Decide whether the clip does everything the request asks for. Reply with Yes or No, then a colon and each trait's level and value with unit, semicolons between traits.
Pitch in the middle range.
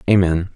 No: very low, 90 Hz